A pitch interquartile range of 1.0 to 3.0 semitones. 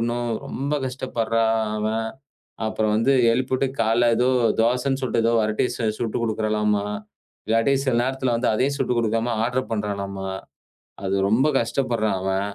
Yes: average, 2.7 semitones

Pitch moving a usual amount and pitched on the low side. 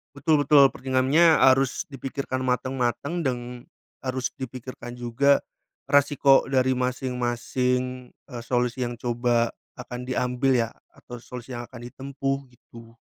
No: narrow, 1.7 semitones; low, 125 Hz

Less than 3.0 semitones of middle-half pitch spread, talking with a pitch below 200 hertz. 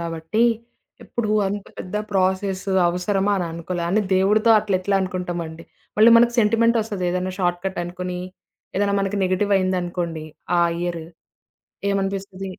Yes: narrow, 2.4 semitones; medium, 185 Hz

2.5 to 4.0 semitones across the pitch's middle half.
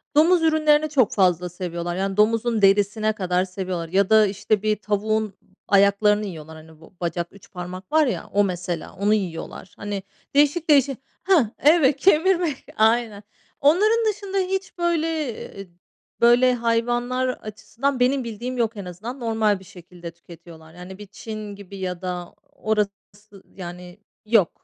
No: wide, 5.6 semitones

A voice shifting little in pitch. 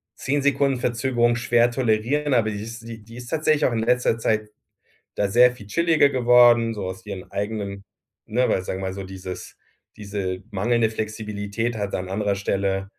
No: average, 3.3 semitones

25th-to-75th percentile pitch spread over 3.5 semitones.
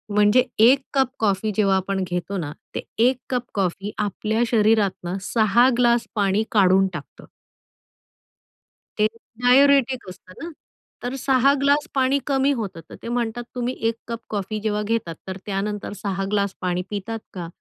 Yes: average, 4.0 semitones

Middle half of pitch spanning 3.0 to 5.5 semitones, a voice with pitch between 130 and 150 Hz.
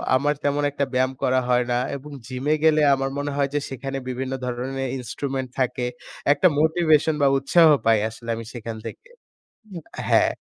No: narrow, 2.5 semitones; low, 135 Hz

